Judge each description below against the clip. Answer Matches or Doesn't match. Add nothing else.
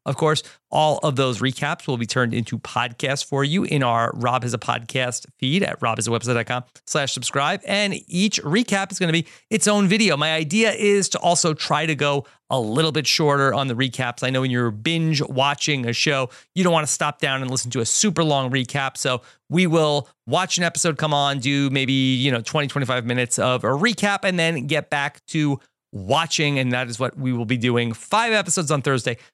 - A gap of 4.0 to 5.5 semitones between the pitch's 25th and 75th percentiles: Matches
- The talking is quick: Matches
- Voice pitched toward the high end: Doesn't match